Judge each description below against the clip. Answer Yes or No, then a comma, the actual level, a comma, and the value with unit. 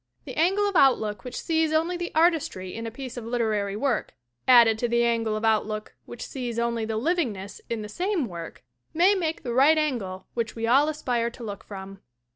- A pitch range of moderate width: No, wide, 6.1 semitones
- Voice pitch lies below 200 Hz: No, high, 235 Hz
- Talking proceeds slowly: No, fast, 205 wpm